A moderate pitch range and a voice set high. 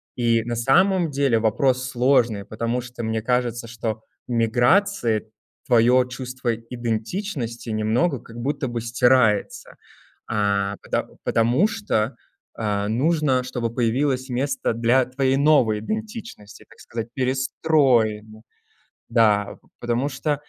No: average, 3.0 semitones; low, 120 Hz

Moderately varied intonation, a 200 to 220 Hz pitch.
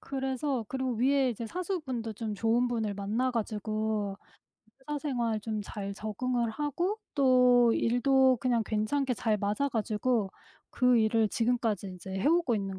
No: average, 3.5 semitones; high, 235 Hz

